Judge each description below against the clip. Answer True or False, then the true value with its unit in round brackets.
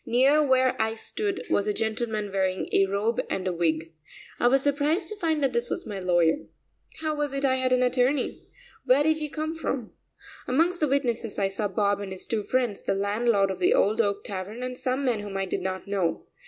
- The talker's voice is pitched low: False (235 Hz)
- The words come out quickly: True (215 wpm)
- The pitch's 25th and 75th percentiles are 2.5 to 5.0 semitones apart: False (5.5 semitones)